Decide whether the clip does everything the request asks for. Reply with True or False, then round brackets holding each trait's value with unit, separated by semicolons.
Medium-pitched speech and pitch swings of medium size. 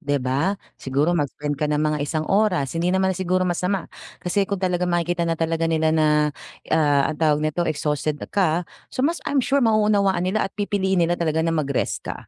True (170 Hz; 3.8 semitones)